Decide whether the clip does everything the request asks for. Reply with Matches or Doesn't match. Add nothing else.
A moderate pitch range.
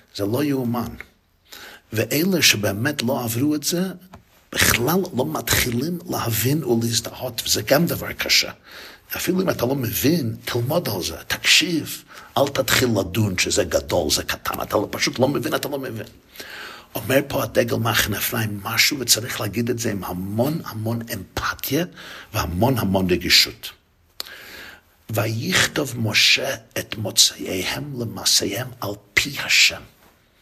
Matches